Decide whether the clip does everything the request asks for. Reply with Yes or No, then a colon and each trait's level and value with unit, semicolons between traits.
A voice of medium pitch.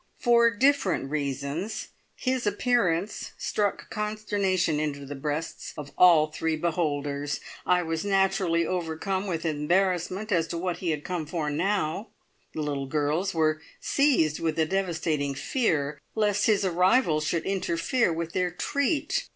Yes: medium, 170 Hz